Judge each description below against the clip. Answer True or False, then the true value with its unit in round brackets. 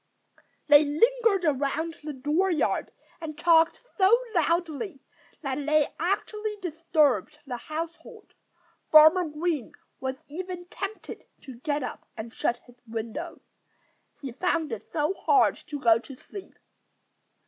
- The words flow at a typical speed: False (125 wpm)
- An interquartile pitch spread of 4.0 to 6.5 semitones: True (4.5 semitones)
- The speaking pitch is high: True (310 Hz)